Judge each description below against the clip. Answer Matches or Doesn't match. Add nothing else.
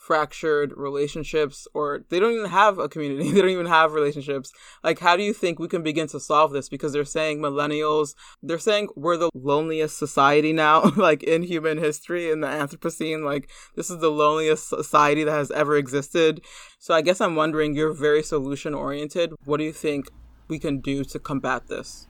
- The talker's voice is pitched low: Doesn't match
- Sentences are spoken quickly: Doesn't match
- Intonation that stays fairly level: Matches